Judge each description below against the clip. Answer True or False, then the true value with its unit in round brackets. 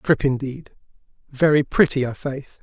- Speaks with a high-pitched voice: False (140 Hz)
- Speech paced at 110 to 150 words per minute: True (135 wpm)